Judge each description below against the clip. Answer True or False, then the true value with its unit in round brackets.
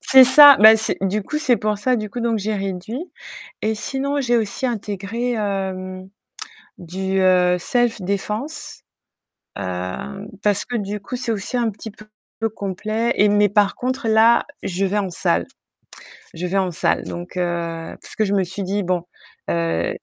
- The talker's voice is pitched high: True (205 Hz)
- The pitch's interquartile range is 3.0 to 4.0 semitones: True (3.7 semitones)